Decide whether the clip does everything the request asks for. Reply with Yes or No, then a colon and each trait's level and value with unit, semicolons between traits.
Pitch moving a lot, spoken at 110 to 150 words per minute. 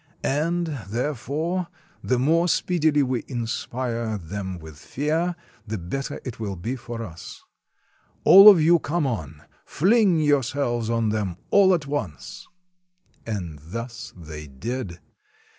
Yes: wide, 7.1 semitones; slow, 135 wpm